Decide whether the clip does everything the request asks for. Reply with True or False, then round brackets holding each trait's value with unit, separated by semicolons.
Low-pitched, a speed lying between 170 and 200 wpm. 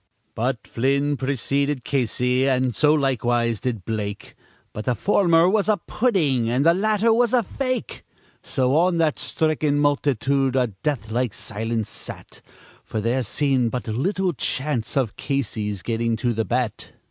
False (130 Hz; 150 wpm)